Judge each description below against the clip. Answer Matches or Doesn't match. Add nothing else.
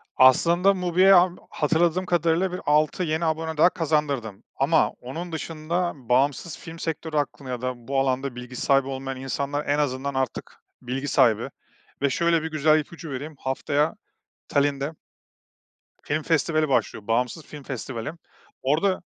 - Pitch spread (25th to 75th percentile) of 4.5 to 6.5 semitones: Doesn't match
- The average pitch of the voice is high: Doesn't match